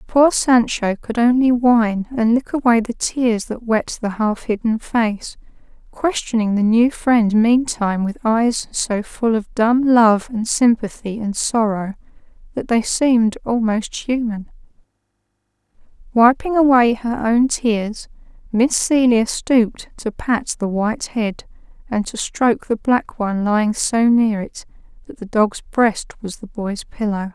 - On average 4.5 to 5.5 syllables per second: No, 4.1 syllables/s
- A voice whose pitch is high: Yes, high, 230 Hz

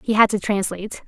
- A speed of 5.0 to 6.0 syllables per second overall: No, 6.4 syllables/s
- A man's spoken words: No, female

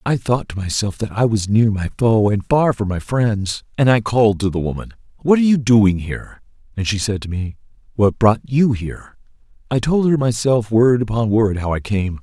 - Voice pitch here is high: No, low, 110 Hz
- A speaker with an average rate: No, fast, 220 wpm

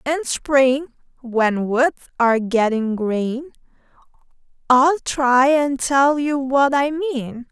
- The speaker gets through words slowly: Yes, slow, 120 wpm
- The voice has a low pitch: No, very high, 265 Hz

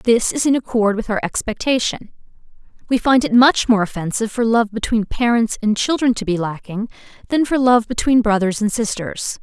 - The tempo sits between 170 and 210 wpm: Yes, average, 185 wpm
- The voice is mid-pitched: No, high, 225 Hz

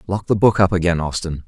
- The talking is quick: Yes, fast, 245 wpm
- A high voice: No, very low, 90 Hz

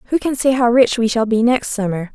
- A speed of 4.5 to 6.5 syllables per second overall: Yes, 5.8 syllables/s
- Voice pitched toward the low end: No, high, 235 Hz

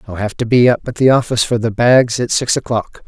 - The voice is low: Yes, low, 120 Hz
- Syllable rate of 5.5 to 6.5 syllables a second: Yes, 5.9 syllables/s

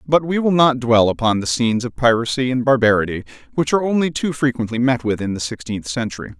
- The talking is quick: Yes, fast, 215 wpm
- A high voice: No, low, 125 Hz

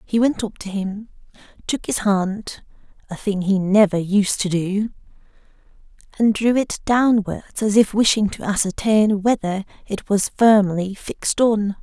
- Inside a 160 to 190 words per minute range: No, average, 150 wpm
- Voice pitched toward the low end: No, high, 205 Hz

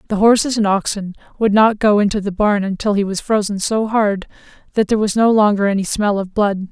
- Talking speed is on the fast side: Yes, fast, 225 wpm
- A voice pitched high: Yes, high, 205 Hz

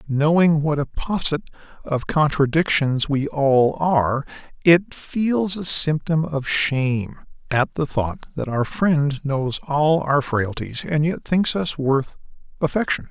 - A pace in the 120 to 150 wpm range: Yes, average, 140 wpm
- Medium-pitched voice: Yes, medium, 150 Hz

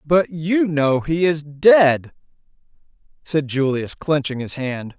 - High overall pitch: No, medium, 150 Hz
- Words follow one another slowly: Yes, slow, 130 wpm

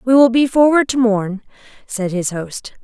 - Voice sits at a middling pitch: No, high, 230 Hz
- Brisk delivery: No, average, 190 wpm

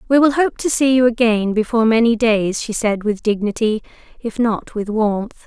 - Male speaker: No, female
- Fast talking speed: No, average, 195 wpm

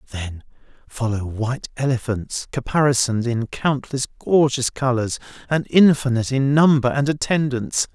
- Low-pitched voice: Yes, low, 130 Hz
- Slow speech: Yes, slow, 115 wpm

